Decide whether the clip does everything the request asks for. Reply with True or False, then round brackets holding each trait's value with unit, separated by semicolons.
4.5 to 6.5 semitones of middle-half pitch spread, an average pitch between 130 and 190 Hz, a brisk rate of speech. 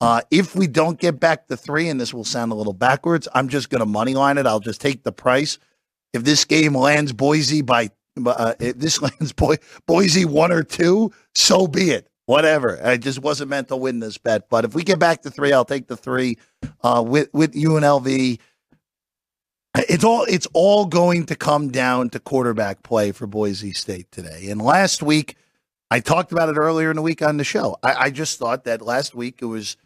True (4.9 semitones; 140 Hz; 210 wpm)